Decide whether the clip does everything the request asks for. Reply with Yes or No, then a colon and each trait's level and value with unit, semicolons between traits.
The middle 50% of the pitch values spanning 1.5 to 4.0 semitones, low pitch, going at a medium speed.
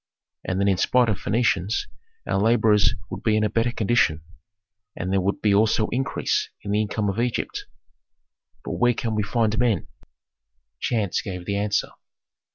Yes: narrow, 2.4 semitones; low, 105 Hz; average, 165 wpm